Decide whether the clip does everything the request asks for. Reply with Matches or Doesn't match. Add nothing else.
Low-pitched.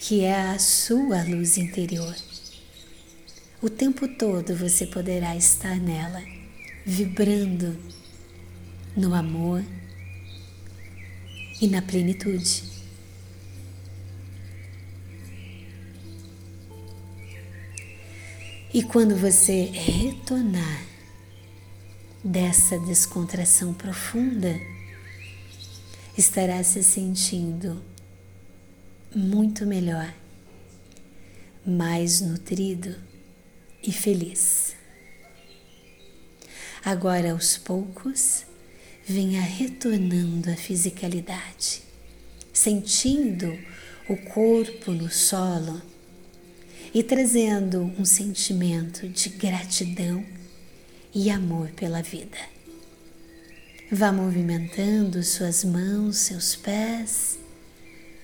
Doesn't match